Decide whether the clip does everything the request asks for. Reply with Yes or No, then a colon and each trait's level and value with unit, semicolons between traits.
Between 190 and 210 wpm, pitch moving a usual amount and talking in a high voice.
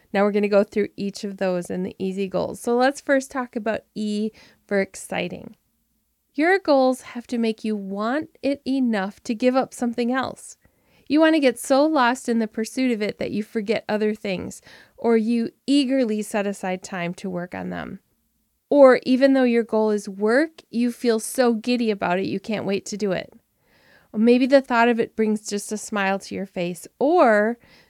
Yes: average, 200 wpm; average, 3.8 semitones; high, 225 Hz